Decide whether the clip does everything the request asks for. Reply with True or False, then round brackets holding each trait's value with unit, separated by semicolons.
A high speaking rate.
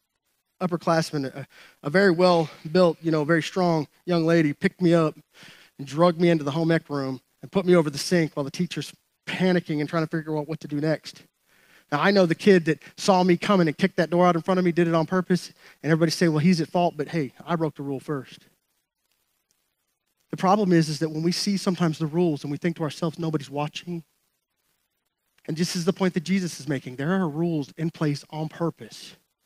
True (230 wpm)